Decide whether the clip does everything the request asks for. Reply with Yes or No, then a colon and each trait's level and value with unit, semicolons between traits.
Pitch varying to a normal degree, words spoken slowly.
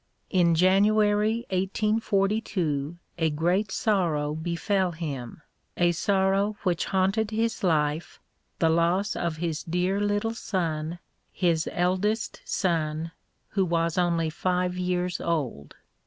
Yes: average, 3.5 semitones; slow, 110 wpm